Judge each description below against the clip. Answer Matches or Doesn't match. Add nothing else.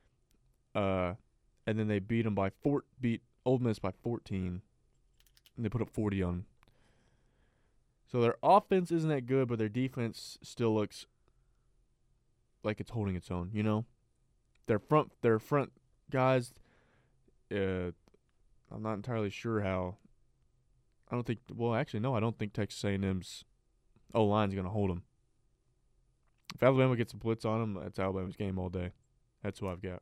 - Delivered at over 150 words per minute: Matches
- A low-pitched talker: Matches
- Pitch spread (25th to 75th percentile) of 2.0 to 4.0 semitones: Matches